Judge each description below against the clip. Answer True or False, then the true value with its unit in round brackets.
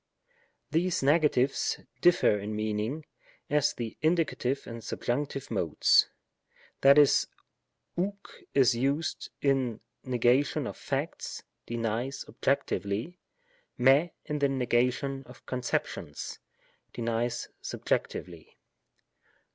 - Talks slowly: True (100 wpm)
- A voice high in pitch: False (130 Hz)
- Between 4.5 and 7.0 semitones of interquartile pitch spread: False (3.7 semitones)